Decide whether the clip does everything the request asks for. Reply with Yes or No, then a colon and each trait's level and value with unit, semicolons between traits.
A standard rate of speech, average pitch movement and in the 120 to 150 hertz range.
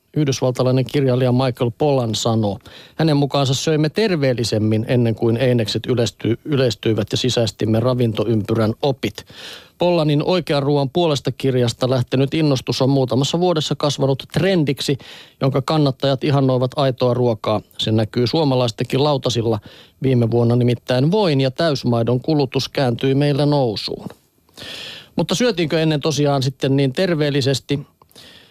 Yes: average, 115 wpm; average, 3.3 semitones; low, 135 Hz